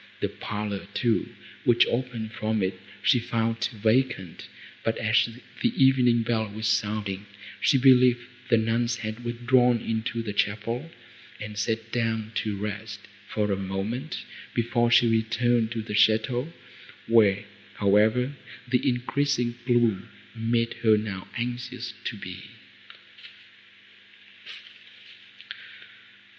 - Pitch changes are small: Yes, narrow, 2.2 semitones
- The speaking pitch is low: Yes, low, 115 Hz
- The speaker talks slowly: Yes, slow, 115 wpm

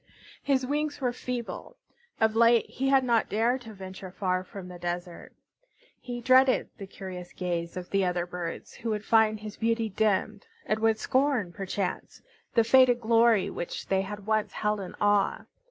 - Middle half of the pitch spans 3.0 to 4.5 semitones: Yes, average, 4.1 semitones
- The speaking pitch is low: No, high, 215 Hz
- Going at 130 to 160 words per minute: No, average, 170 wpm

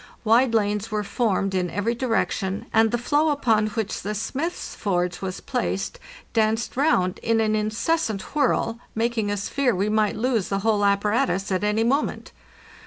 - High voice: Yes, high, 215 Hz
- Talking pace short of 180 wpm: Yes, average, 165 wpm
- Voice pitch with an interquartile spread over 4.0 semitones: No, average, 2.8 semitones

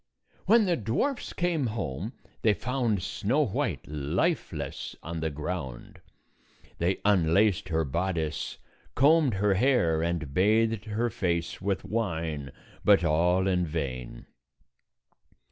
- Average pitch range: No, wide, 5.9 semitones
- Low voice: Yes, very low, 95 Hz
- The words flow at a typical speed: No, slow, 120 wpm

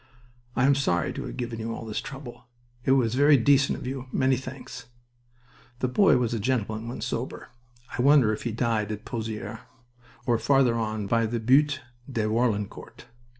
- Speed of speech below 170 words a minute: No, average, 180 wpm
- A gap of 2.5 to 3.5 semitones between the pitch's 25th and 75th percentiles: Yes, average, 3.1 semitones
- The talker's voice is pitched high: No, low, 120 Hz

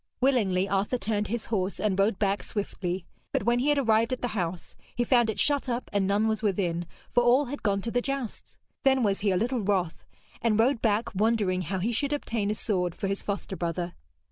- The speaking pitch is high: Yes, high, 215 Hz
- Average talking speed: No, fast, 220 wpm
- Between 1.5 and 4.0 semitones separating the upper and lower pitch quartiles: Yes, average, 3.7 semitones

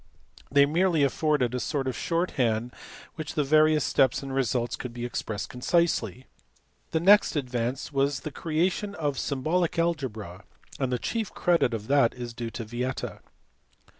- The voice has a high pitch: No, low, 135 Hz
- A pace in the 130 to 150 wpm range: No, average, 165 wpm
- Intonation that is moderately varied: Yes, average, 4.5 semitones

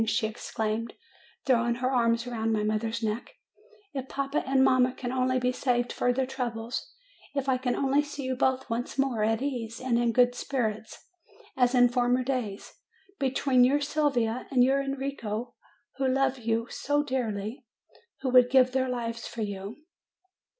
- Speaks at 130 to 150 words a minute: No, average, 165 wpm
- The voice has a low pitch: No, very high, 250 Hz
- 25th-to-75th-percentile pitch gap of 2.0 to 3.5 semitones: Yes, narrow, 2.4 semitones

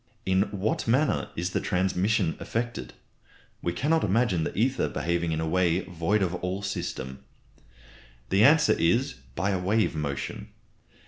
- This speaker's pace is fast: No, average, 145 wpm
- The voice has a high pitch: No, very low, 95 Hz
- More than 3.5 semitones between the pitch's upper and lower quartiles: Yes, average, 4.4 semitones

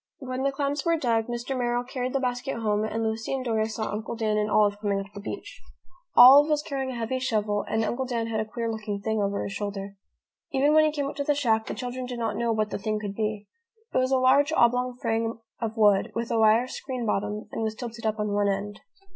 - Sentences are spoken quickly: Yes, fast, 245 wpm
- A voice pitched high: Yes, high, 230 Hz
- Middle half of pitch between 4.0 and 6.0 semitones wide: No, average, 3.2 semitones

